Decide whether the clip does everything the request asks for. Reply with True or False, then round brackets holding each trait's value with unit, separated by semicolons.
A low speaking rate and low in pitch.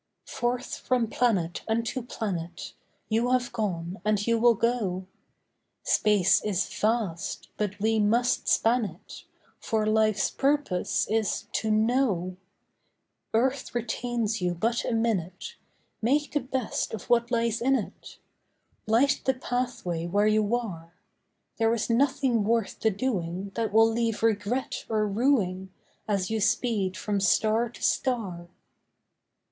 False (130 wpm; 220 Hz)